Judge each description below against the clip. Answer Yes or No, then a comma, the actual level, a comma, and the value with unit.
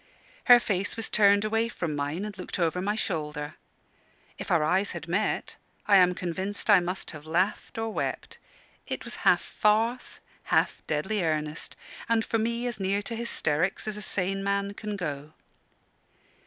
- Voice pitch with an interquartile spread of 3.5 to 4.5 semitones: Yes, average, 4.2 semitones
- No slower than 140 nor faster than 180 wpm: Yes, average, 170 wpm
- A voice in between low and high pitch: No, high, 195 Hz